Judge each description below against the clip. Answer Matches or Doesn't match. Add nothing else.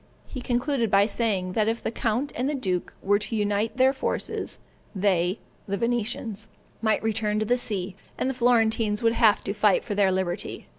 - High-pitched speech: Matches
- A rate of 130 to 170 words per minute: Doesn't match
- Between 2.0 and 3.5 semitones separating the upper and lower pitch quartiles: Matches